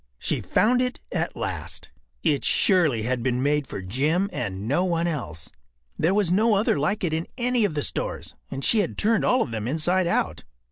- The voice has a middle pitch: Yes, medium, 165 Hz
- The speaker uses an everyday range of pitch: No, wide, 7.4 semitones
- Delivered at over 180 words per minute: Yes, average, 200 wpm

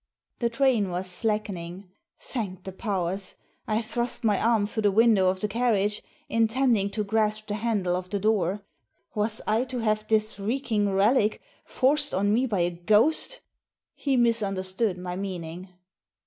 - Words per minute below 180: Yes, average, 155 wpm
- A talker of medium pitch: No, high, 210 Hz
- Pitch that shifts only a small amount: No, average, 3.1 semitones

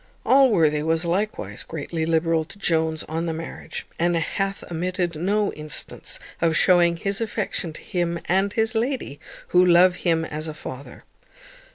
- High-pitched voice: No, medium, 170 Hz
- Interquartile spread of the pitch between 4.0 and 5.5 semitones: No, average, 3.4 semitones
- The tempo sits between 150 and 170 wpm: Yes, average, 155 wpm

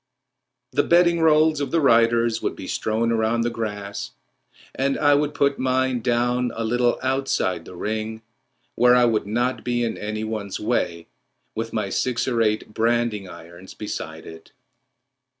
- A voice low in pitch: Yes, low, 115 Hz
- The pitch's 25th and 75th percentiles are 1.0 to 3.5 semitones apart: Yes, average, 3.0 semitones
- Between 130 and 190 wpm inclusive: Yes, average, 160 wpm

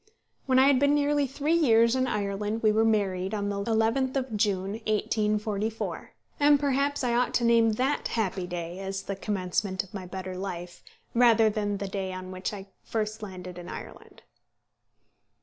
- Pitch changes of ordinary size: Yes, average, 3.8 semitones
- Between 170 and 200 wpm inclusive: Yes, average, 175 wpm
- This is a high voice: Yes, high, 215 Hz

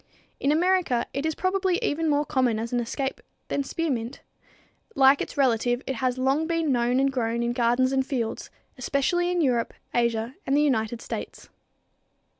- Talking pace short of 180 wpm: Yes, average, 170 wpm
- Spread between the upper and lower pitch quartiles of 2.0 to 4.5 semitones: Yes, average, 3.8 semitones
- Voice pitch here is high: Yes, very high, 265 Hz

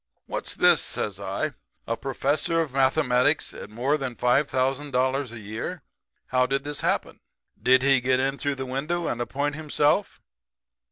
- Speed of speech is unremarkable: Yes, average, 155 wpm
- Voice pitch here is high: No, low, 135 Hz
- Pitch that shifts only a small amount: Yes, narrow, 2.3 semitones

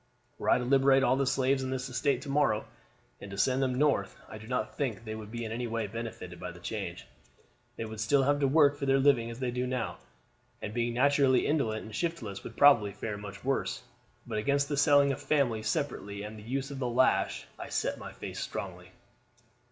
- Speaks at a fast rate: Yes, fast, 225 wpm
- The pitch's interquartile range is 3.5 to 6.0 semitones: Yes, average, 4.0 semitones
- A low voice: Yes, low, 125 Hz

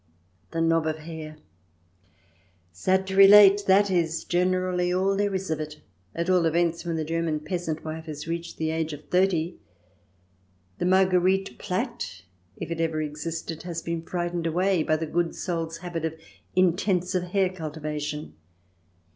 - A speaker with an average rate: Yes, average, 155 wpm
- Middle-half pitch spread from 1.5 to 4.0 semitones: Yes, narrow, 2.4 semitones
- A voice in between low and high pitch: Yes, medium, 170 Hz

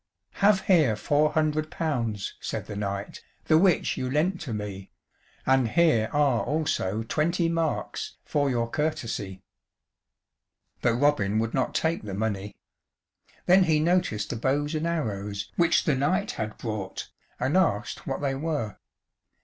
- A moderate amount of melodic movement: No, wide, 6.6 semitones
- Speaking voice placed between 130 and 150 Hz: Yes, medium, 140 Hz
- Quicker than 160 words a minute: No, average, 145 wpm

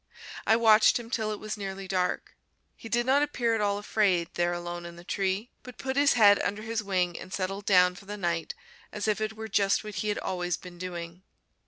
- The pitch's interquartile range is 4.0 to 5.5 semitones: No, average, 3.3 semitones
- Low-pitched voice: No, high, 200 Hz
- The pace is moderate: No, fast, 225 wpm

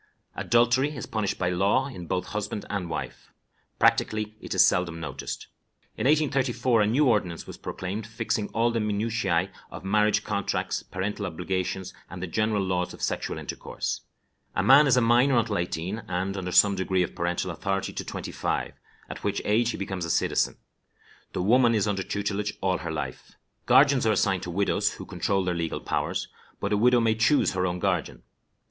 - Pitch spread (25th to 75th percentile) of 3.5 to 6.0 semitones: Yes, average, 3.9 semitones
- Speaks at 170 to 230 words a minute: Yes, average, 185 wpm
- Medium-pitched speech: No, low, 100 Hz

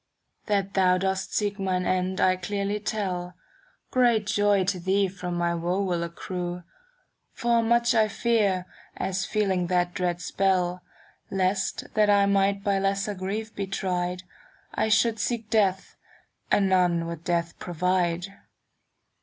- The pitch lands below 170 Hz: No, high, 190 Hz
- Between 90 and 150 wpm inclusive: Yes, average, 145 wpm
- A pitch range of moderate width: No, narrow, 2.3 semitones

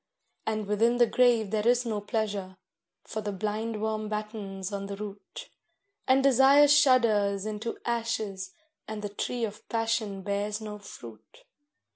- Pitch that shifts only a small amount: Yes, narrow, 2.3 semitones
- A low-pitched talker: No, high, 215 Hz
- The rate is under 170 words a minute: Yes, average, 140 wpm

